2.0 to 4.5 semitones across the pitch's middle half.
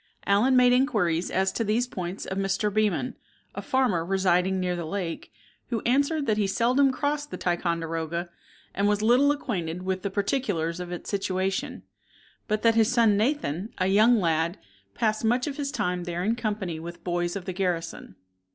No: average, 5.1 semitones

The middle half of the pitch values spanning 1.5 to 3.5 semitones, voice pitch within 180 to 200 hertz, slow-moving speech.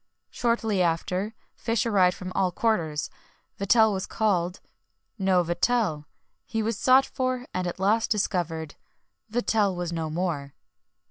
No: average, 4.3 semitones; high, 190 Hz; slow, 130 wpm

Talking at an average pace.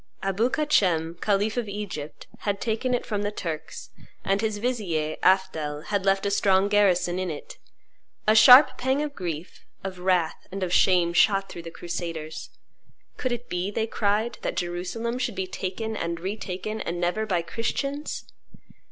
Yes: average, 165 wpm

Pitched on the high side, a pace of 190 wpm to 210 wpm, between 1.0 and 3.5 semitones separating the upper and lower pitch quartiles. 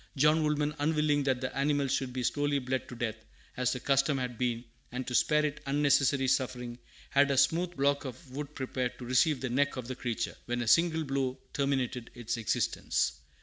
No: low, 135 Hz; average, 195 wpm; narrow, 2.6 semitones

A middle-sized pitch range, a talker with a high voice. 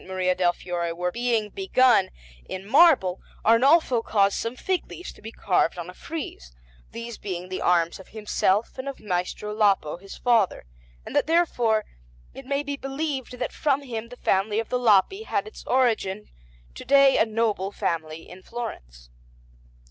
No: wide, 5.8 semitones; high, 220 Hz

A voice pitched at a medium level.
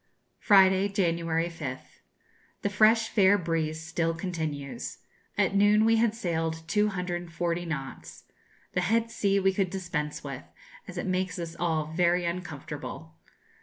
Yes: medium, 175 Hz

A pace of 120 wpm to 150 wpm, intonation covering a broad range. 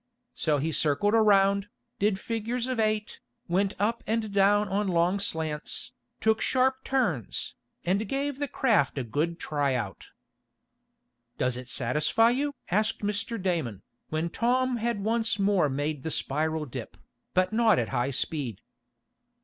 Yes: average, 140 wpm; wide, 6.9 semitones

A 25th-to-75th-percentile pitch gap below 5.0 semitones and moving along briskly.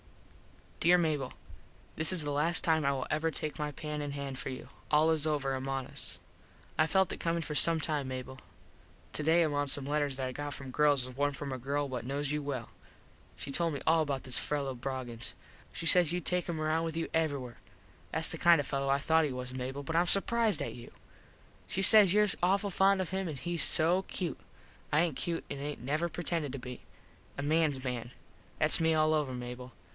Yes: average, 3.3 semitones; fast, 220 wpm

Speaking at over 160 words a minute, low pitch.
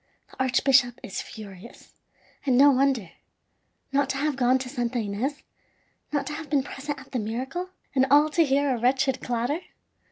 No: average, 170 wpm; very high, 265 Hz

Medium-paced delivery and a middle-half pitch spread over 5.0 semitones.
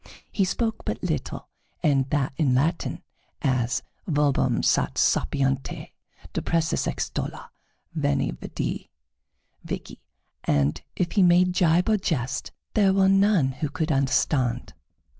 No: slow, 120 wpm; wide, 5.4 semitones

